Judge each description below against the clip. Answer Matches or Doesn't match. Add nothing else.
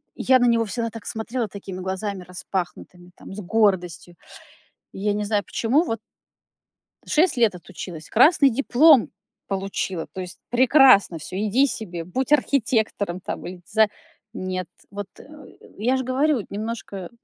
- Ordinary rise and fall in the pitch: Matches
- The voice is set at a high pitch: Matches